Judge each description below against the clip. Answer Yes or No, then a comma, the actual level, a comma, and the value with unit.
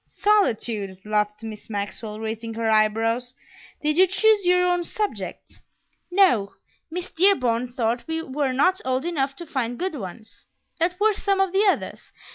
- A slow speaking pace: No, average, 155 wpm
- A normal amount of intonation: No, wide, 8.3 semitones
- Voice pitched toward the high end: Yes, very high, 260 Hz